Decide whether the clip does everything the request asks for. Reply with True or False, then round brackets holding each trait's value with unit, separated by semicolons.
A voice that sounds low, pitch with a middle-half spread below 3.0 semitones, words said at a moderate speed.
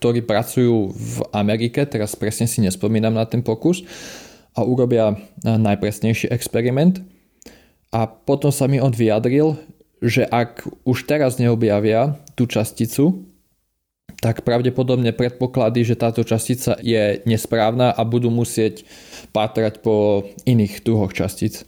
True (115 Hz; 2.4 semitones; 120 wpm)